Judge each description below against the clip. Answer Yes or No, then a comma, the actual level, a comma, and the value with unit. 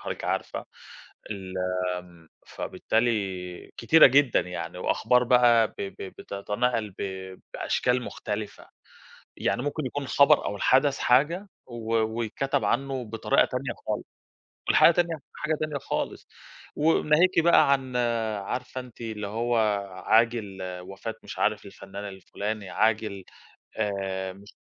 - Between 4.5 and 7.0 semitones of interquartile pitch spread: Yes, average, 4.9 semitones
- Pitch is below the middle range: Yes, low, 115 Hz